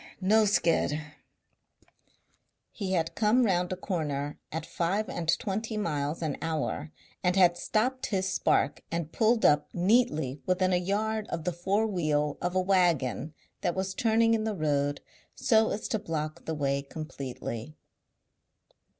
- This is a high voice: No, medium, 175 Hz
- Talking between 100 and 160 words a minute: Yes, average, 150 wpm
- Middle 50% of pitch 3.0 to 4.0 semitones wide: No, average, 5.2 semitones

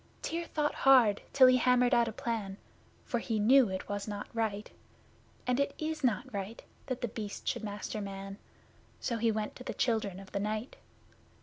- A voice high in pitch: Yes, high, 225 Hz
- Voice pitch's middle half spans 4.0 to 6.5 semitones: No, average, 3.6 semitones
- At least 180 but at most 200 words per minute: Yes, average, 190 wpm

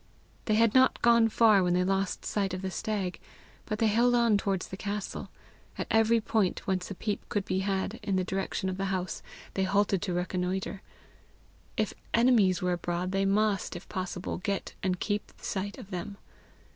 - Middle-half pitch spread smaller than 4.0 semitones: Yes, narrow, 2.4 semitones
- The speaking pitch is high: Yes, high, 195 Hz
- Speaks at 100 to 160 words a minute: No, average, 185 wpm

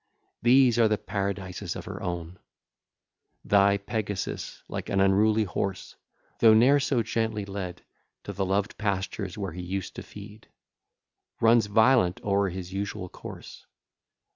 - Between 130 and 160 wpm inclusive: Yes, average, 140 wpm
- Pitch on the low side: Yes, low, 100 Hz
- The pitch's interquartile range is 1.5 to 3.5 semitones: Yes, narrow, 2.4 semitones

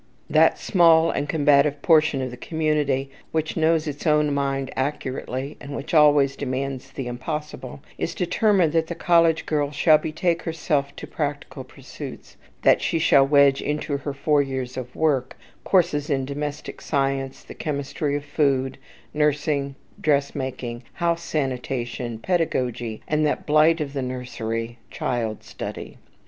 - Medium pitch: Yes, medium, 145 Hz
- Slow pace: No, average, 145 wpm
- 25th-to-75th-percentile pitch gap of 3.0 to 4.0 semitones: No, narrow, 2.6 semitones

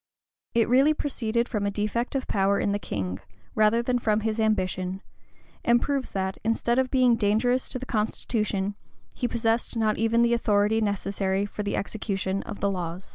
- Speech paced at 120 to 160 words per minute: No, average, 180 wpm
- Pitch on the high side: Yes, high, 215 Hz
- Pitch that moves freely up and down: No, average, 2.9 semitones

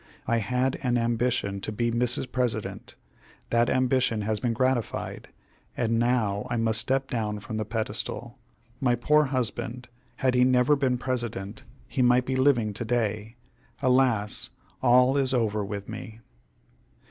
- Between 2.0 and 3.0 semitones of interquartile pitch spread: Yes, narrow, 2.6 semitones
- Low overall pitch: Yes, low, 120 Hz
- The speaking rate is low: No, average, 145 wpm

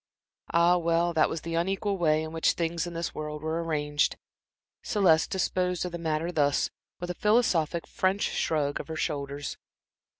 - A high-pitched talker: No, medium, 165 Hz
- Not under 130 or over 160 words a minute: No, average, 170 wpm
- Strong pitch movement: No, narrow, 2.4 semitones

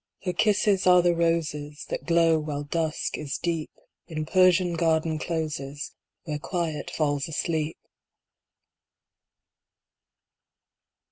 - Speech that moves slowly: Yes, slow, 105 wpm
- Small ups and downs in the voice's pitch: Yes, narrow, 2.3 semitones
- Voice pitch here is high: No, medium, 160 Hz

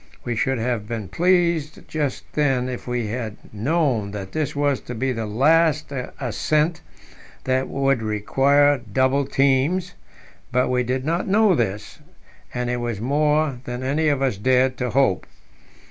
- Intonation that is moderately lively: Yes, average, 3.5 semitones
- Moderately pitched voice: No, low, 130 Hz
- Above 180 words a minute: No, average, 155 wpm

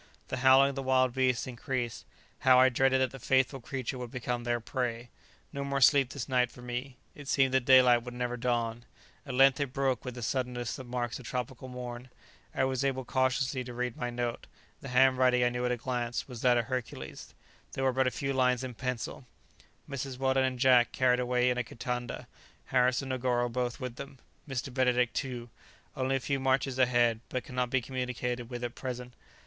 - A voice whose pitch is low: Yes, low, 125 Hz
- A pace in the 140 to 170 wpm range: No, fast, 205 wpm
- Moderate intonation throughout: No, narrow, 1.3 semitones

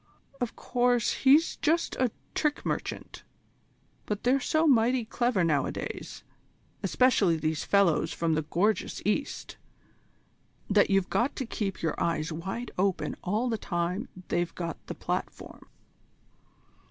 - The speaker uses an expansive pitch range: Yes, wide, 6.4 semitones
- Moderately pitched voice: No, high, 210 Hz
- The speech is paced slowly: Yes, slow, 130 wpm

